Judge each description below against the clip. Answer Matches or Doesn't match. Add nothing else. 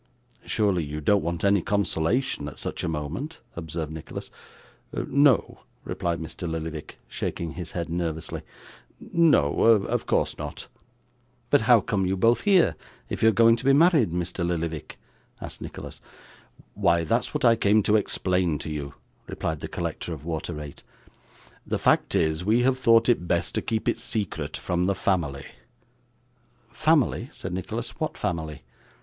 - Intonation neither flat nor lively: Doesn't match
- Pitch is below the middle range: Matches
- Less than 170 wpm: Matches